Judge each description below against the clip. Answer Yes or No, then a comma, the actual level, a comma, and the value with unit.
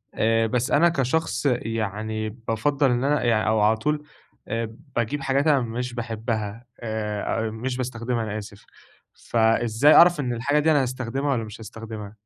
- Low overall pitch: Yes, low, 115 Hz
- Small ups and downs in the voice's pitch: No, average, 3.5 semitones